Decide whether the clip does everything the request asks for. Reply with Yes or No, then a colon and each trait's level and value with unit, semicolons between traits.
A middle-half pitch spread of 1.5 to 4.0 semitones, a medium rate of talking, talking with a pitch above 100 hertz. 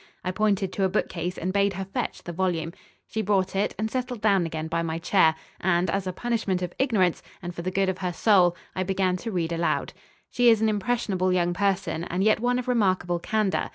No: average, 2.9 semitones; fast, 225 wpm; high, 190 Hz